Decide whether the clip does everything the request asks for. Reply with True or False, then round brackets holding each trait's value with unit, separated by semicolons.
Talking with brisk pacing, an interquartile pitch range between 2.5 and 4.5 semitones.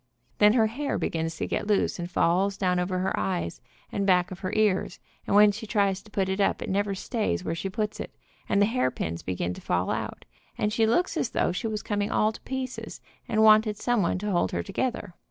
True (225 wpm; 3.2 semitones)